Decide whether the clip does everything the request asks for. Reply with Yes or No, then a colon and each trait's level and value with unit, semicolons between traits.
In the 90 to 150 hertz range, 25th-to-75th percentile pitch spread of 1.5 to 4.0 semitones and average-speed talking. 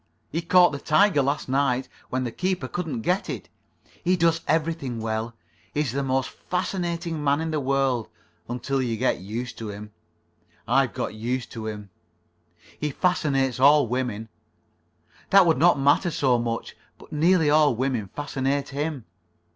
No: medium, 140 Hz; average, 4.8 semitones; average, 155 wpm